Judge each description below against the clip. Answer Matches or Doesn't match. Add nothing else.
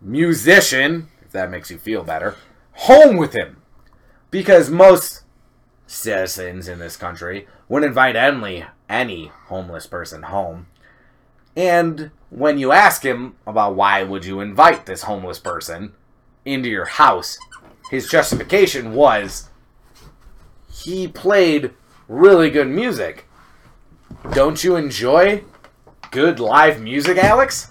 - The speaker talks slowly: Matches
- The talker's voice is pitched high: Doesn't match